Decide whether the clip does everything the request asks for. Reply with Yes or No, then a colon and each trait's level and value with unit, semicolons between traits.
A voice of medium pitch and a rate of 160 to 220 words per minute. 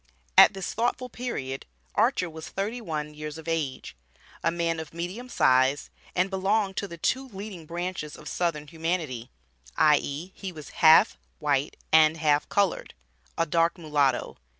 No: medium, 165 Hz; average, 150 wpm